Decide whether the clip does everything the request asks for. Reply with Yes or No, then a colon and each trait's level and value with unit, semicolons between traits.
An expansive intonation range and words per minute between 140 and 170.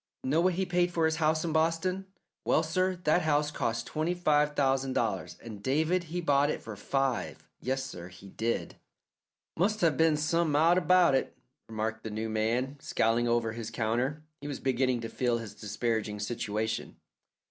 No: wide, 6.0 semitones; average, 180 wpm